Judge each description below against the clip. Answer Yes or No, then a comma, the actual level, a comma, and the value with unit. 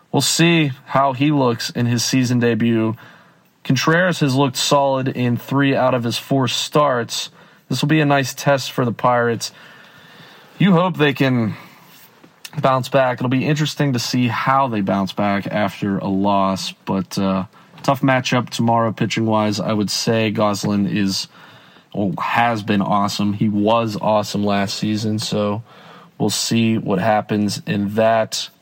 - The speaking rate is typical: Yes, average, 155 wpm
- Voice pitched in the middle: No, low, 120 Hz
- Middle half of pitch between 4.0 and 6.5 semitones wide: Yes, average, 4.6 semitones